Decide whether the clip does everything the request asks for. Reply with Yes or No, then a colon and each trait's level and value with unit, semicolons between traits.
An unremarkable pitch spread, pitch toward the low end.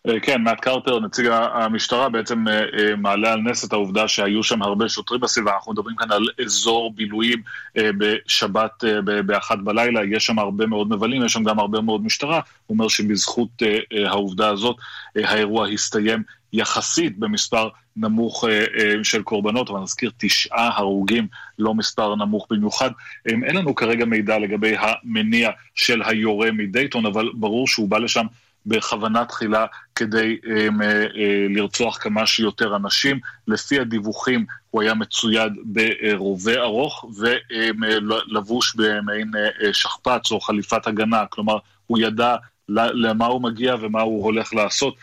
No: narrow, 1.3 semitones; low, 110 Hz